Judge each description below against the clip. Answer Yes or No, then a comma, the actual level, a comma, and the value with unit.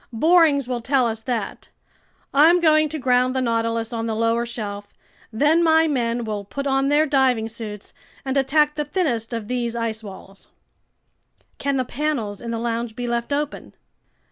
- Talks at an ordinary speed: Yes, average, 170 wpm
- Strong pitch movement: No, average, 4.0 semitones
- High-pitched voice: Yes, high, 245 Hz